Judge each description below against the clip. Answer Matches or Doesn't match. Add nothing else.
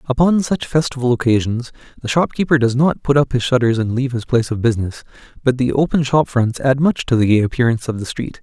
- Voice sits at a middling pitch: Doesn't match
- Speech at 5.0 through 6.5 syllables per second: Matches